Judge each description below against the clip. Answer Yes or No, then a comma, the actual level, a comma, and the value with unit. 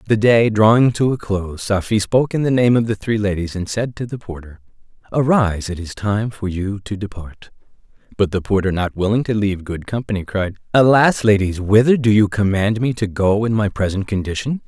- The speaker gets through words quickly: Yes, fast, 210 wpm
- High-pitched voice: No, low, 105 Hz